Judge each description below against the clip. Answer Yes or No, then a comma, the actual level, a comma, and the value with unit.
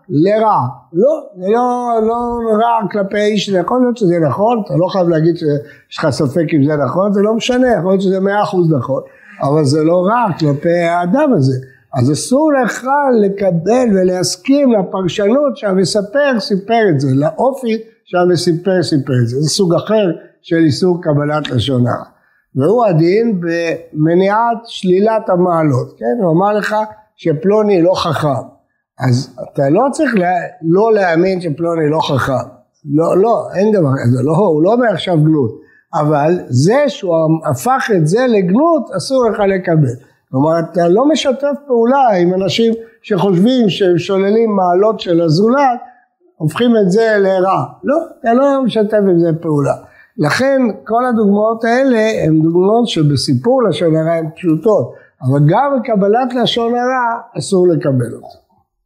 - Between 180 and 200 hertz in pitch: Yes, high, 190 Hz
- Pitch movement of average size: No, wide, 6.0 semitones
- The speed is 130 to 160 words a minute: Yes, average, 150 wpm